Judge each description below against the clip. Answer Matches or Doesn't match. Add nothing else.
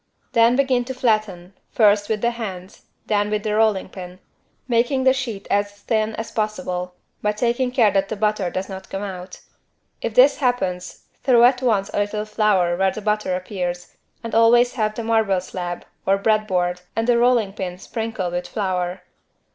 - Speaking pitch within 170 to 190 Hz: Doesn't match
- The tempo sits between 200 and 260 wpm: Doesn't match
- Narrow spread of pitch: Doesn't match